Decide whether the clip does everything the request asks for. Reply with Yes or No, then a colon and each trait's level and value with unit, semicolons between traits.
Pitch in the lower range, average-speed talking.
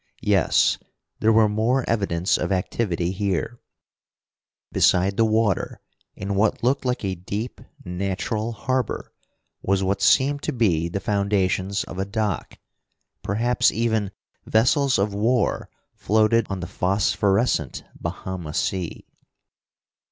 No: low, 100 Hz; slow, 120 wpm